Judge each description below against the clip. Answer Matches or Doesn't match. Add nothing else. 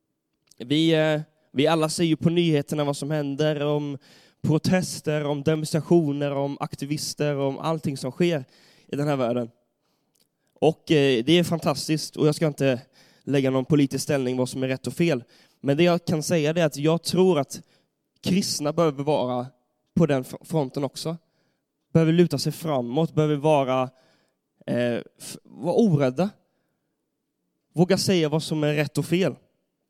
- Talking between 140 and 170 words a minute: Matches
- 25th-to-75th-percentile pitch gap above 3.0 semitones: Doesn't match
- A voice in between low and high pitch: Matches